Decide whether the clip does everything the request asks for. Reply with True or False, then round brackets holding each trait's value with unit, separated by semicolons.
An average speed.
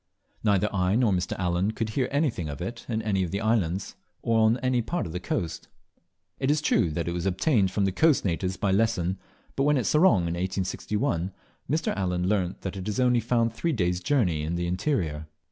False (215 wpm)